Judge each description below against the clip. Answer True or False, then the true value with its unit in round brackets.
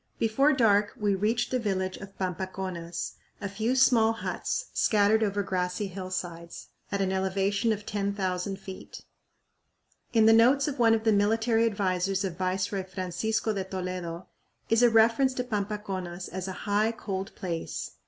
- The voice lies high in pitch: True (200 Hz)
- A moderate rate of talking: True (155 wpm)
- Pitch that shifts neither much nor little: True (3.0 semitones)